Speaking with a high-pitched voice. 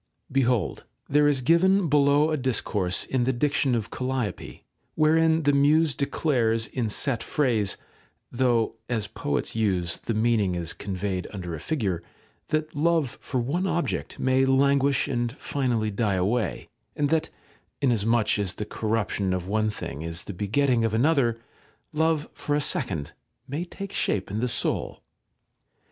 No: low, 125 Hz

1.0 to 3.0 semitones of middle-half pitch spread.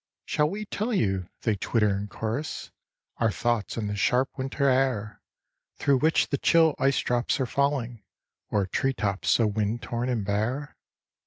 No: average, 4.7 semitones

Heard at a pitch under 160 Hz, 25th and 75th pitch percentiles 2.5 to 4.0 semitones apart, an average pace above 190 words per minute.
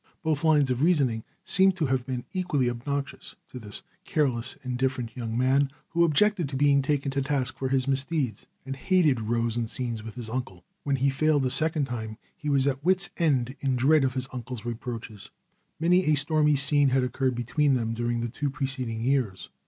Yes: low, 135 Hz; average, 3.3 semitones; average, 200 wpm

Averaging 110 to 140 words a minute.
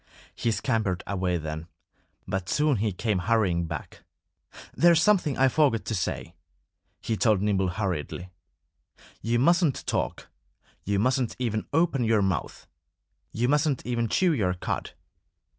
Yes: slow, 135 wpm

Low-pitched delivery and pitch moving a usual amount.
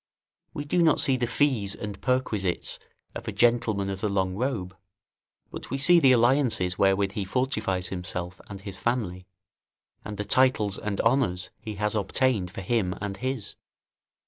Yes: low, 105 Hz; average, 4.8 semitones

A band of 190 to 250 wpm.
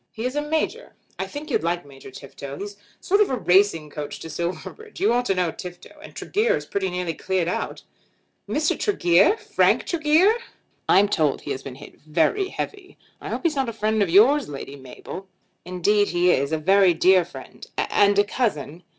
Yes: average, 195 wpm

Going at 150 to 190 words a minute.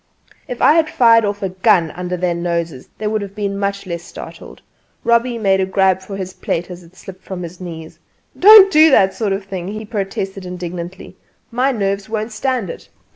No: fast, 205 wpm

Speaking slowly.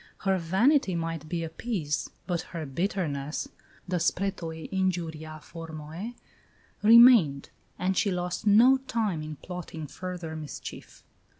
Yes: slow, 115 wpm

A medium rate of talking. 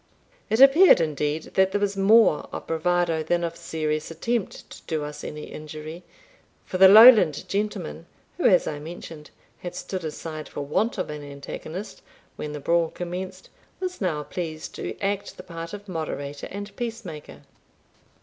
Yes: average, 160 wpm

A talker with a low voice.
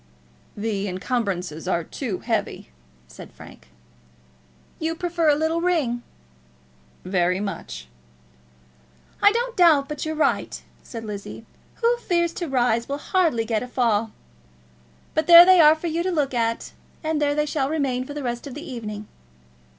No: very high, 275 Hz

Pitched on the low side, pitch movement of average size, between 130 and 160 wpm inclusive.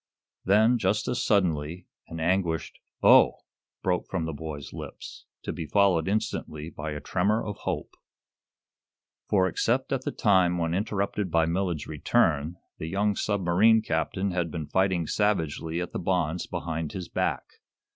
Yes: very low, 90 Hz; average, 3.7 semitones; average, 150 wpm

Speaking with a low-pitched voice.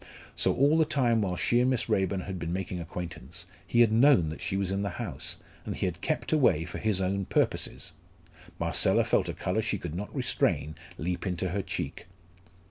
Yes: very low, 95 Hz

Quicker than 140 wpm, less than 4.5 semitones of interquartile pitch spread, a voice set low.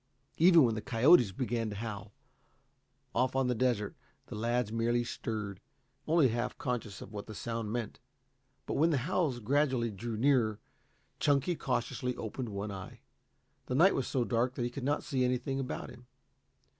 Yes: average, 170 wpm; average, 3.2 semitones; low, 120 Hz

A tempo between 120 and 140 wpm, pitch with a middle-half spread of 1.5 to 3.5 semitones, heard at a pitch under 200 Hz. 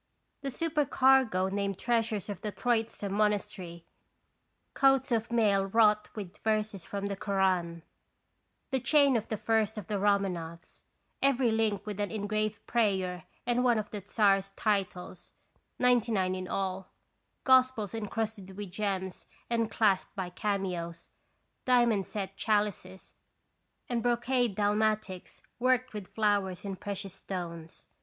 No: slow, 135 wpm; average, 3.0 semitones; high, 210 Hz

